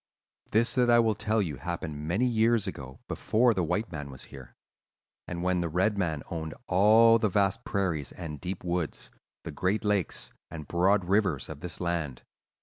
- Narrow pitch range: No, average, 5.2 semitones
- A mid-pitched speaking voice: No, very low, 90 Hz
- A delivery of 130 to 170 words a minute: No, average, 180 wpm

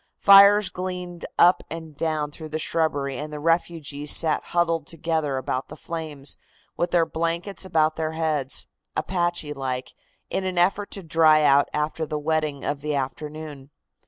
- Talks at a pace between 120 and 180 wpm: Yes, average, 160 wpm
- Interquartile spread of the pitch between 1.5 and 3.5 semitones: Yes, narrow, 2.6 semitones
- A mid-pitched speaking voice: Yes, medium, 160 Hz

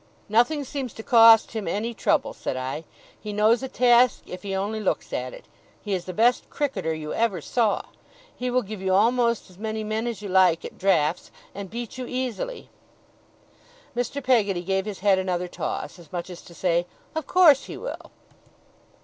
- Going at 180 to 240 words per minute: Yes, average, 190 wpm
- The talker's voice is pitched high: Yes, high, 215 Hz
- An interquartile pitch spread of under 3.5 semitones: No, average, 4.6 semitones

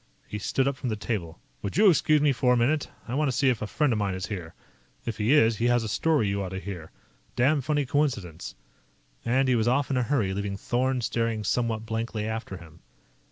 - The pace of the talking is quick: Yes, fast, 235 wpm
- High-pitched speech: No, low, 115 Hz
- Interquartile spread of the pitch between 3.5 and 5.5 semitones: Yes, average, 4.5 semitones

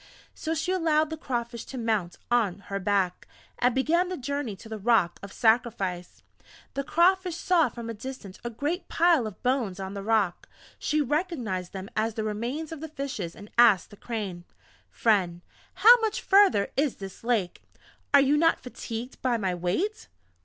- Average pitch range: No, wide, 7.3 semitones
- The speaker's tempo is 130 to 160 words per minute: No, average, 175 wpm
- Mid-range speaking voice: No, high, 235 Hz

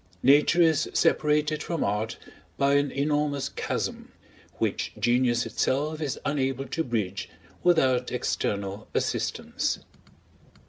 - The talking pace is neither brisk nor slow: No, slow, 105 wpm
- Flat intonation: No, average, 3.9 semitones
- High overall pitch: No, medium, 140 Hz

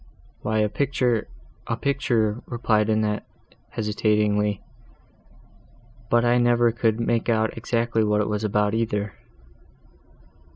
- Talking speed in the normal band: No, slow, 100 wpm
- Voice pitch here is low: Yes, low, 110 Hz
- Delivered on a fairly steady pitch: Yes, narrow, 2.0 semitones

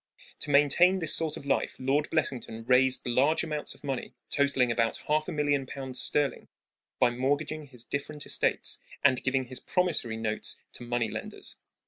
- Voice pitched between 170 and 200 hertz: No, medium, 140 Hz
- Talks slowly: No, average, 165 wpm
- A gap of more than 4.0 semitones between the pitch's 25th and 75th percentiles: No, average, 3.1 semitones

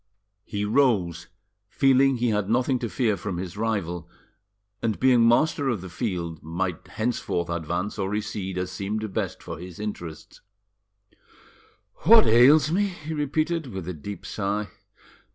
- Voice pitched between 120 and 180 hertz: No, low, 105 Hz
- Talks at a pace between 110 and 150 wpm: Yes, average, 145 wpm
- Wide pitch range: Yes, wide, 5.8 semitones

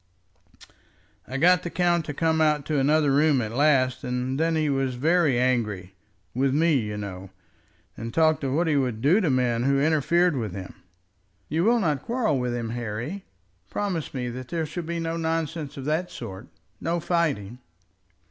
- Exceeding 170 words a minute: Yes, average, 180 wpm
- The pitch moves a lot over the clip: No, average, 4.8 semitones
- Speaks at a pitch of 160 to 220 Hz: No, medium, 145 Hz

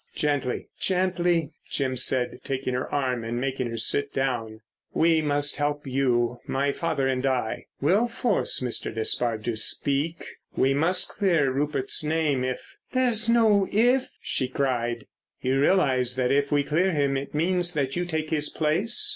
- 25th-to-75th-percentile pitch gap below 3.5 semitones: No, average, 4.6 semitones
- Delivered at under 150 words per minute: No, average, 155 wpm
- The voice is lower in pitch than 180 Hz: Yes, medium, 140 Hz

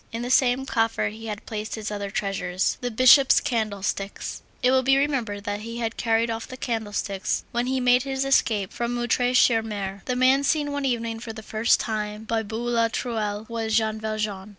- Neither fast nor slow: Yes, average, 195 wpm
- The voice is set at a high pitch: Yes, high, 225 Hz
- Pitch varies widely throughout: No, narrow, 2.6 semitones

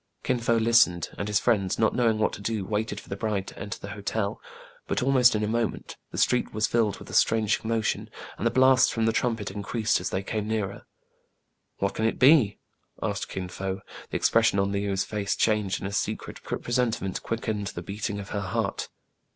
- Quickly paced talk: Yes, fast, 220 wpm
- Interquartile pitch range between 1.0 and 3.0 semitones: Yes, narrow, 2.5 semitones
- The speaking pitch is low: Yes, low, 105 Hz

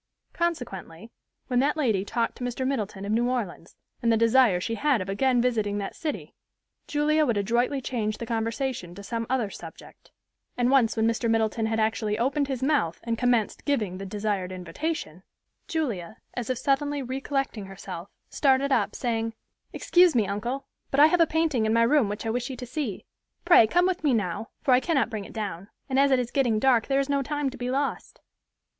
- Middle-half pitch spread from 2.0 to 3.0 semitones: No, average, 4.2 semitones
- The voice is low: No, high, 240 Hz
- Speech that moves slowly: No, average, 200 wpm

